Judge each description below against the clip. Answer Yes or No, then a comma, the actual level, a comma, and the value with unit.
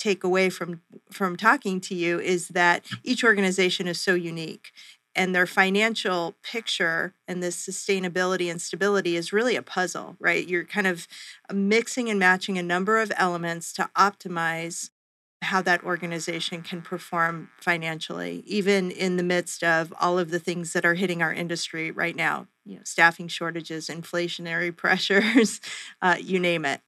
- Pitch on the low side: No, medium, 180 Hz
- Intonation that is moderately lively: No, narrow, 2.1 semitones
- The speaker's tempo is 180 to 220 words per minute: No, average, 160 wpm